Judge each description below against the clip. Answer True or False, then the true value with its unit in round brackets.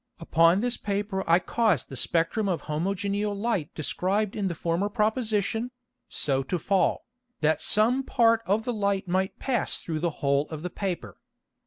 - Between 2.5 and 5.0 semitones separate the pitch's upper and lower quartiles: True (4.4 semitones)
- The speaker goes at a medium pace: True (165 wpm)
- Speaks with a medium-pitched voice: False (195 Hz)